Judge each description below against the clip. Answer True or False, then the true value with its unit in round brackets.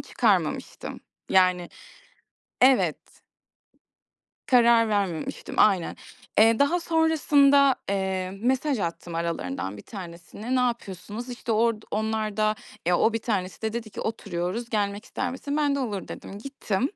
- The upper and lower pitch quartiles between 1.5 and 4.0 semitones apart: False (4.8 semitones)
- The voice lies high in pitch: True (220 Hz)